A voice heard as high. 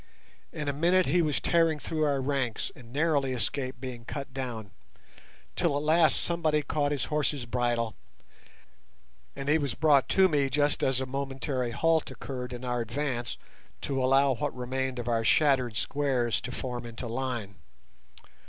No: low, 135 Hz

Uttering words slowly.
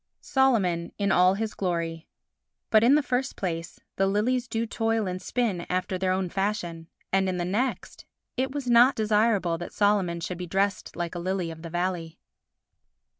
No: average, 175 wpm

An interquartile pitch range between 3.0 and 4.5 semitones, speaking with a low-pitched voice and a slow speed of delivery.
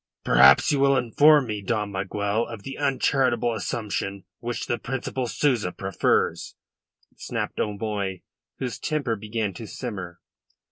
Yes: average, 4.2 semitones; low, 110 Hz; slow, 130 wpm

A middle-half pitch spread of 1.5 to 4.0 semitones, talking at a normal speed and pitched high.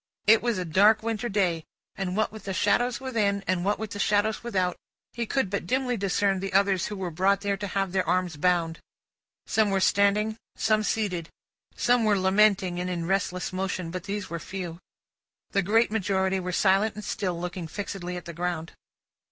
Yes: average, 2.7 semitones; average, 195 wpm; high, 195 Hz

